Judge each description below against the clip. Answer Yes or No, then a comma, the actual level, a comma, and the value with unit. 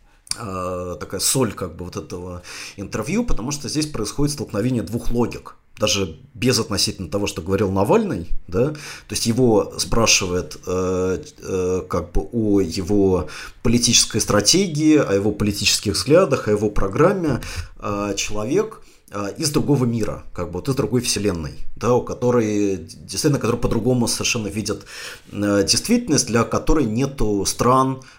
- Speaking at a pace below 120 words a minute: No, average, 130 wpm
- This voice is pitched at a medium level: No, low, 105 Hz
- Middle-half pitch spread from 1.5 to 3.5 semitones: No, average, 4.2 semitones